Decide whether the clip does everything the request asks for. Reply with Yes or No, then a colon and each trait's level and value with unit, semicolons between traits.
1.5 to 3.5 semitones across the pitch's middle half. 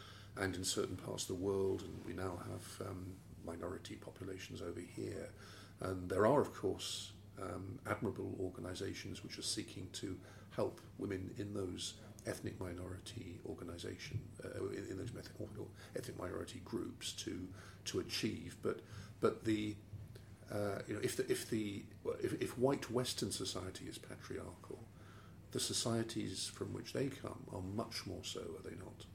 Yes: narrow, 2.4 semitones